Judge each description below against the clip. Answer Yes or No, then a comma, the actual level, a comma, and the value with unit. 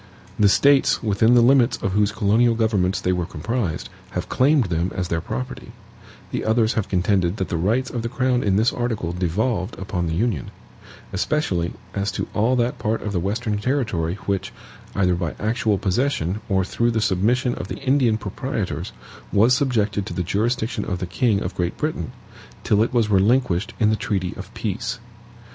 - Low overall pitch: Yes, low, 105 Hz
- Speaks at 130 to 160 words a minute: No, average, 185 wpm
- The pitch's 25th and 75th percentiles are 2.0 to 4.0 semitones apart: No, average, 4.6 semitones